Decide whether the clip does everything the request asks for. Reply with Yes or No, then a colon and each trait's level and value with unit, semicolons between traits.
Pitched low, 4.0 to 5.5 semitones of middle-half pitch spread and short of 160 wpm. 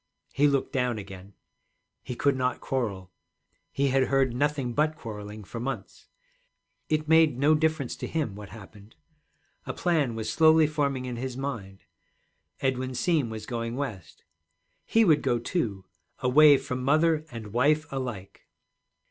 Yes: low, 130 Hz; average, 4.7 semitones; average, 150 wpm